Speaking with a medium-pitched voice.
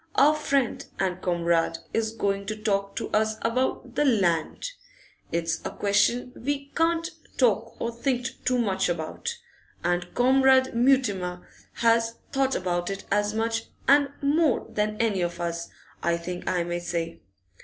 No: high, 220 Hz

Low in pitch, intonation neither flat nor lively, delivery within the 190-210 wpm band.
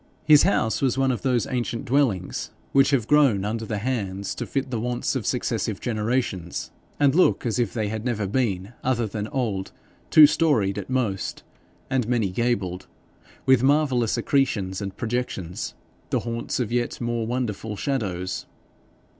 No: low, 120 Hz; average, 4.2 semitones; average, 160 wpm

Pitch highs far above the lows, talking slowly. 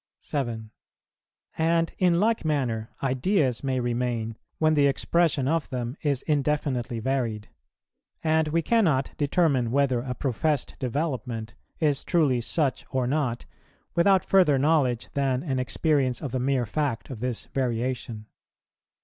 No: average, 4.0 semitones; slow, 130 wpm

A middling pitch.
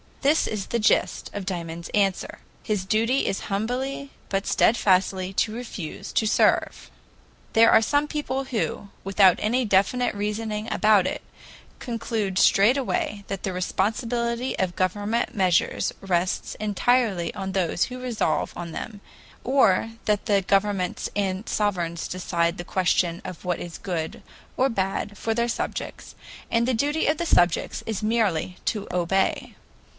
No: high, 205 Hz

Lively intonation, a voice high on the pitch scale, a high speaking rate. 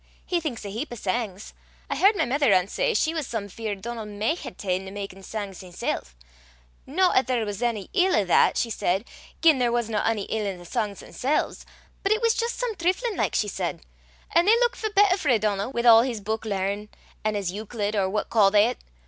Yes: wide, 7.4 semitones; high, 225 Hz; fast, 225 wpm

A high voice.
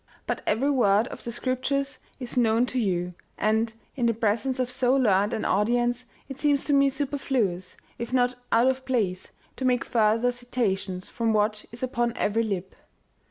Yes: high, 240 Hz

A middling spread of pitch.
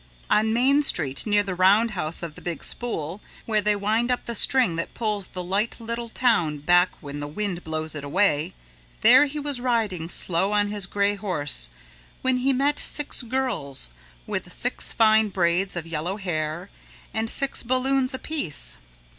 No: wide, 5.9 semitones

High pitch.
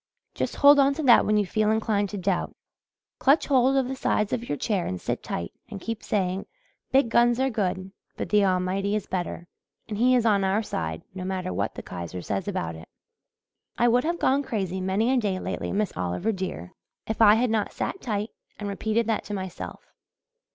Yes: high, 210 Hz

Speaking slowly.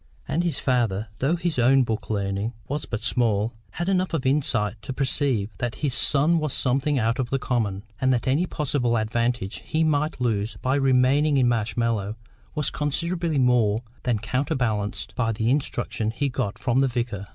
No: average, 175 wpm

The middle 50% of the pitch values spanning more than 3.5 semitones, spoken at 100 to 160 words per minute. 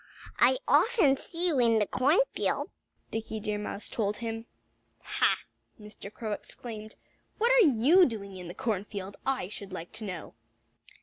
Yes: average, 4.9 semitones; average, 150 wpm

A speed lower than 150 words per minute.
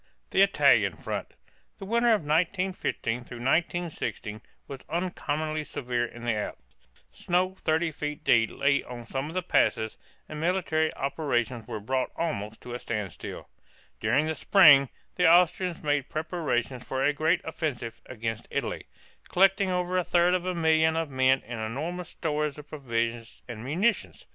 No: average, 155 wpm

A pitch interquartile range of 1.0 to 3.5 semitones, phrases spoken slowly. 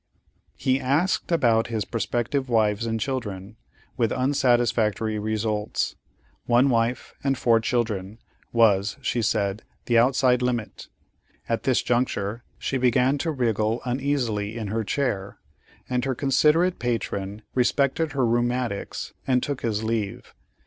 Yes: average, 3.0 semitones; slow, 130 wpm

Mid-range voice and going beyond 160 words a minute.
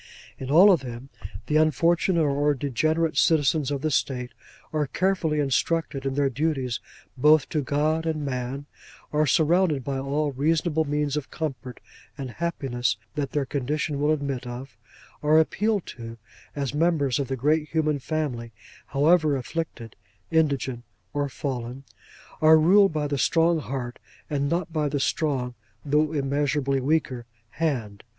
No: medium, 145 Hz; average, 145 wpm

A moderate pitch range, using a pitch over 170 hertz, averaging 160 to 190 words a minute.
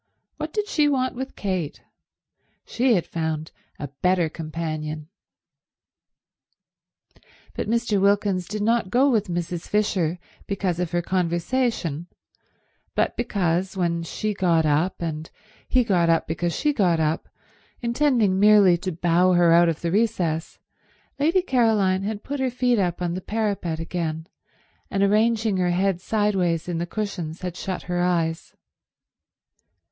No: average, 4.2 semitones; medium, 185 Hz; average, 140 wpm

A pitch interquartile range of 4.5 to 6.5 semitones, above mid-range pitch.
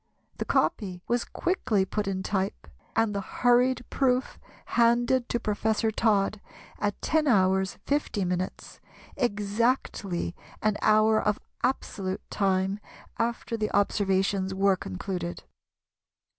No: average, 3.6 semitones; high, 210 Hz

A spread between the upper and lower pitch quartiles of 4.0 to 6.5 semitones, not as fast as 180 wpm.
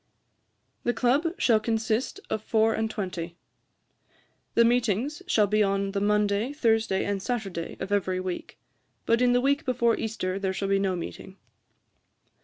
No: average, 3.3 semitones; average, 160 wpm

